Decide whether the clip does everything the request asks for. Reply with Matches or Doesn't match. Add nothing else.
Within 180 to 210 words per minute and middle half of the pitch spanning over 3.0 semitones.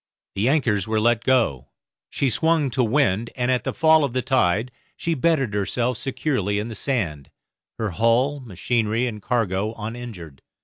Doesn't match